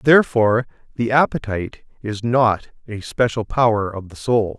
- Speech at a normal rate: Yes, average, 145 wpm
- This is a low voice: Yes, low, 115 Hz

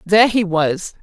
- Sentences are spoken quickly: No, average, 175 wpm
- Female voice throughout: Yes, female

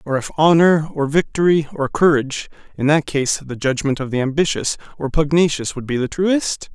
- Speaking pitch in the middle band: Yes, medium, 150 Hz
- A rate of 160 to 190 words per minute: Yes, average, 185 wpm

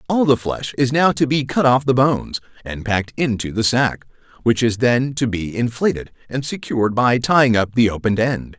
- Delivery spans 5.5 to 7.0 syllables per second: No, 5.1 syllables/s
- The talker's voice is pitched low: Yes, low, 120 Hz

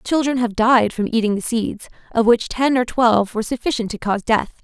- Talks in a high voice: Yes, high, 235 Hz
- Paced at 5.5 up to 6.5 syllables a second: Yes, 5.6 syllables/s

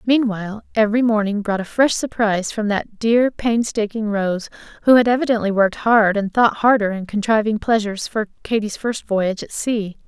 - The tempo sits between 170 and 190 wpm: Yes, average, 175 wpm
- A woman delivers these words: Yes, female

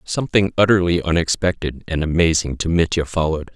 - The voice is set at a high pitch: No, very low, 85 Hz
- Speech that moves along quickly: No, slow, 135 wpm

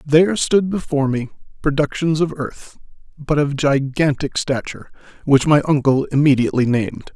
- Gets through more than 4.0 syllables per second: Yes, 5.3 syllables/s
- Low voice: No, medium, 145 Hz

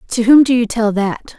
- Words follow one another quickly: Yes, fast, 260 wpm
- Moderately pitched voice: No, high, 230 Hz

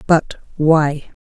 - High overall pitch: No, medium, 155 Hz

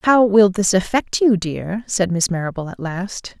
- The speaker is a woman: Yes, female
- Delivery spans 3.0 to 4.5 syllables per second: Yes, 4.3 syllables/s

